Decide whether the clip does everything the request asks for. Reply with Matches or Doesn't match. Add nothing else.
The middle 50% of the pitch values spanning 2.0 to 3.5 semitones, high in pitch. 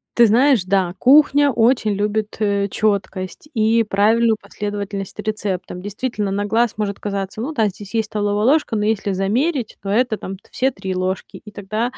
Matches